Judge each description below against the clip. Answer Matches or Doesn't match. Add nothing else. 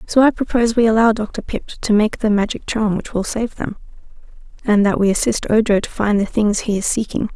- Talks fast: Matches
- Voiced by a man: Doesn't match